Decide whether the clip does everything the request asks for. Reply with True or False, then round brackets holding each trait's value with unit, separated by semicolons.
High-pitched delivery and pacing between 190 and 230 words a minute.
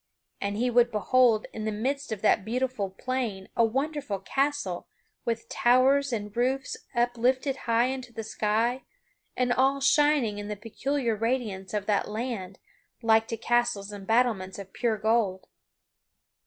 False (230 Hz; 150 wpm)